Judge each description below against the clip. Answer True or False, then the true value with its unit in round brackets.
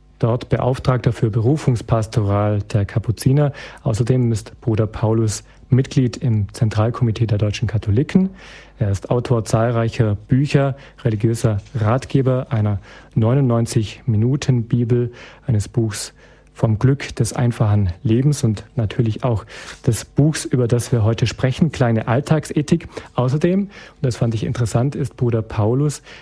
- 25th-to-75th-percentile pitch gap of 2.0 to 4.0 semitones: True (3.1 semitones)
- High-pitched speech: False (120 Hz)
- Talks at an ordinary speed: False (120 wpm)